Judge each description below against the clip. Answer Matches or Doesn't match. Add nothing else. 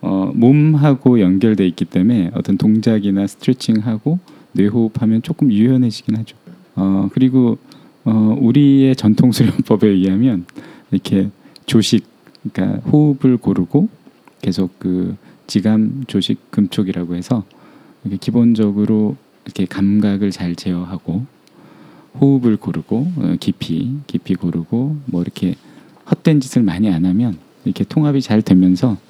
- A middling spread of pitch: Matches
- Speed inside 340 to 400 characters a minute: Doesn't match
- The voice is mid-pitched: Doesn't match